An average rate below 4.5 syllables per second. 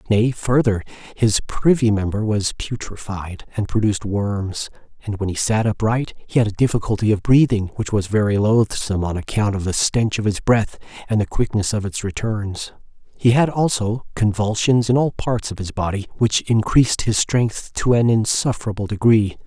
No: 5.0 syllables/s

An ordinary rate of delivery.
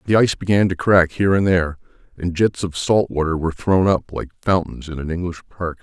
No: fast, 225 wpm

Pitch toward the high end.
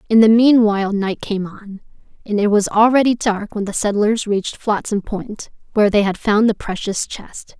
Yes: high, 210 Hz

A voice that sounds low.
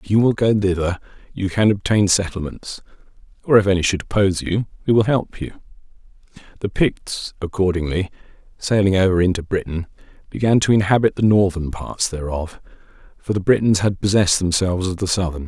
Yes: very low, 95 Hz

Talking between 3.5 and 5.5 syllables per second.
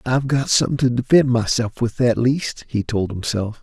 Yes: 5.1 syllables/s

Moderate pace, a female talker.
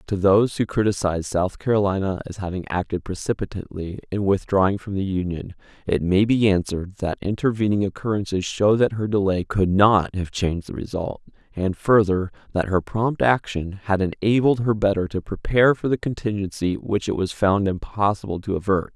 No: average, 170 wpm; male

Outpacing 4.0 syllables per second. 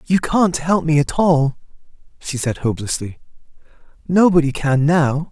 Yes: 4.6 syllables/s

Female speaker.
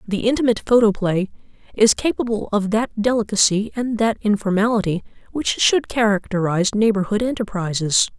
Yes: female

